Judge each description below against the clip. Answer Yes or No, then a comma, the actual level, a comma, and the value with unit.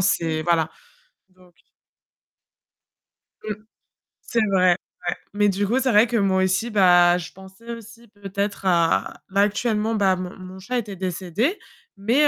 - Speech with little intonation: No, average, 3.1 semitones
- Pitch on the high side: Yes, high, 195 Hz